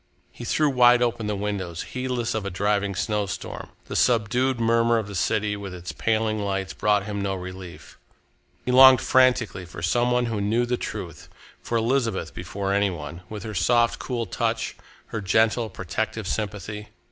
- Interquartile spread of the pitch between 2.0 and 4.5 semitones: Yes, average, 3.2 semitones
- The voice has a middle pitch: No, low, 105 Hz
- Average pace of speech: Yes, average, 170 wpm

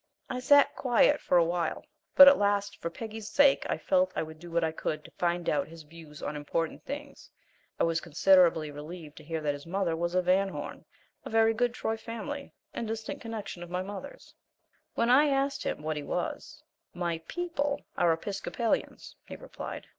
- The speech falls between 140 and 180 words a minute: No, average, 190 wpm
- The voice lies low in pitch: No, medium, 185 Hz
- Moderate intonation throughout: No, wide, 6.4 semitones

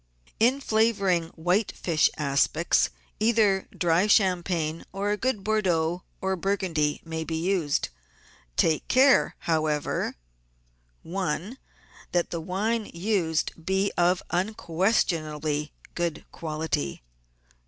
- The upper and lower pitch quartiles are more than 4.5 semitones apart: No, average, 3.9 semitones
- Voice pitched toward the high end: No, medium, 175 Hz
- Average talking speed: No, slow, 110 wpm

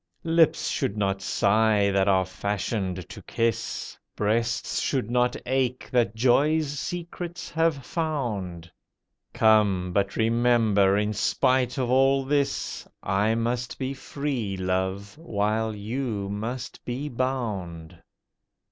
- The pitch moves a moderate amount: Yes, average, 4.7 semitones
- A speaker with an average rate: No, slow, 115 wpm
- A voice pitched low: Yes, low, 115 Hz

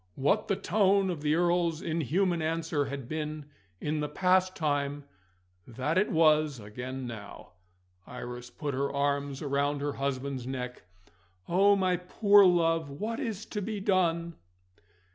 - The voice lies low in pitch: No, medium, 155 Hz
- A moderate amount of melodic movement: Yes, average, 4.6 semitones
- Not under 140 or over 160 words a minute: Yes, average, 145 wpm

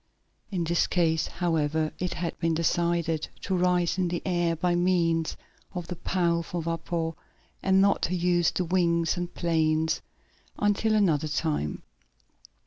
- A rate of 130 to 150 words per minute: Yes, average, 140 wpm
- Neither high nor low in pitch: Yes, medium, 170 Hz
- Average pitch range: No, narrow, 1.6 semitones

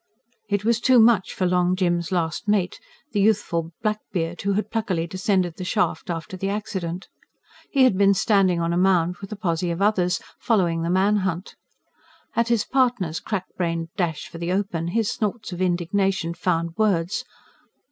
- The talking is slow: No, average, 175 wpm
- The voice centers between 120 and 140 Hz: No, medium, 185 Hz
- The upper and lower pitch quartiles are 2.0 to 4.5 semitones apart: Yes, average, 3.4 semitones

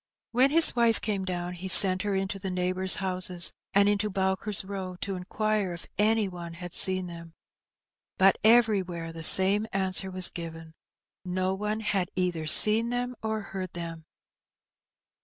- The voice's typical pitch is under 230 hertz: Yes, high, 190 Hz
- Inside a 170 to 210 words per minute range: No, average, 160 wpm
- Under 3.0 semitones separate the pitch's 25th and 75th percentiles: Yes, narrow, 2.6 semitones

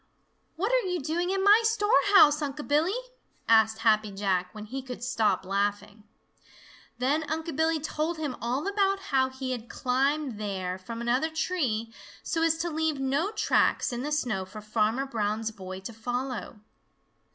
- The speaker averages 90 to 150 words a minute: No, average, 165 wpm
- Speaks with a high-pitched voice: Yes, very high, 260 Hz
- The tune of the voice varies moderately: No, wide, 6.7 semitones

